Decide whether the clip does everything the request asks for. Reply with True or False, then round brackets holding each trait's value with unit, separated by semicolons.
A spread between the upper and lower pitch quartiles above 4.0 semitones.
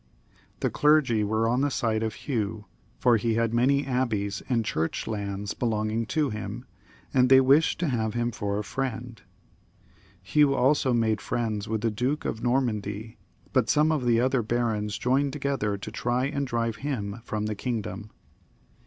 False (3.4 semitones)